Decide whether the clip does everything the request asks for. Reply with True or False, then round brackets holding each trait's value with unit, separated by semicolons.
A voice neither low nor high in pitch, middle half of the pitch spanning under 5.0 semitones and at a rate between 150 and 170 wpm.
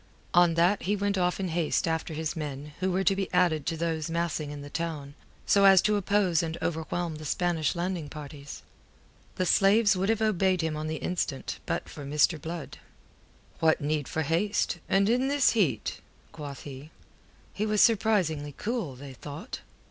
False (170 Hz; 4.2 semitones; 180 wpm)